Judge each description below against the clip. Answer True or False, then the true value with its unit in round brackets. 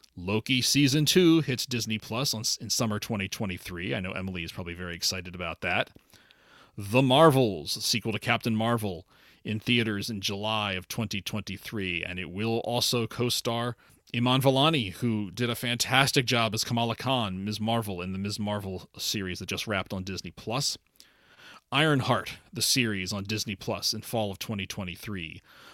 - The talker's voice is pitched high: False (110 Hz)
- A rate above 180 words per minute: False (165 wpm)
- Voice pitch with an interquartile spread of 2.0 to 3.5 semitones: False (3.9 semitones)